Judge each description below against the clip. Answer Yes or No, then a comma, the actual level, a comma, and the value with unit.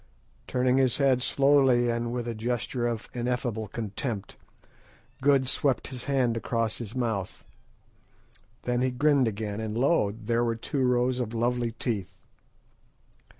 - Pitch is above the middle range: No, low, 120 Hz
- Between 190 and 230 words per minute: No, average, 140 wpm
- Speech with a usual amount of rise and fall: No, narrow, 2.1 semitones